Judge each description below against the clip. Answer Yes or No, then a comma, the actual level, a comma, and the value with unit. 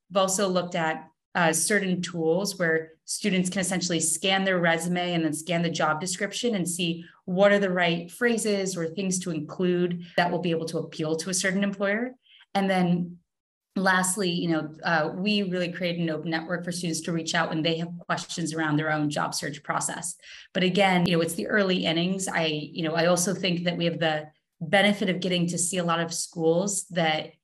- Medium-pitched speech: Yes, medium, 175 Hz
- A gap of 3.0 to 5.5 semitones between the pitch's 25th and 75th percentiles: No, narrow, 2.5 semitones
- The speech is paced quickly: Yes, fast, 210 wpm